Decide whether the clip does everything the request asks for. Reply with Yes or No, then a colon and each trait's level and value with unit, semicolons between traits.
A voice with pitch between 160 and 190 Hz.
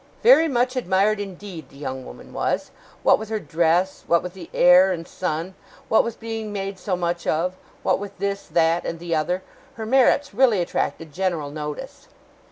Yes: medium, 185 Hz